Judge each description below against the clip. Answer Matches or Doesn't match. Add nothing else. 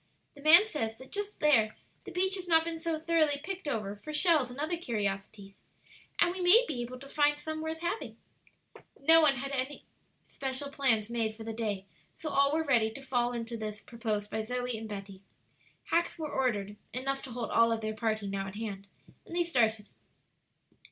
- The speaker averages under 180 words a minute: Doesn't match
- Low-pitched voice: Doesn't match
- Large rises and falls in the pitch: Matches